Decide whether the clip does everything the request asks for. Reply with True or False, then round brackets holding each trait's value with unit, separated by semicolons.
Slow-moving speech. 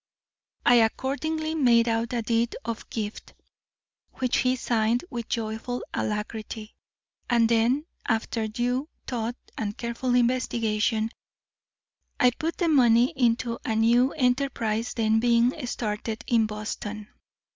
True (120 wpm)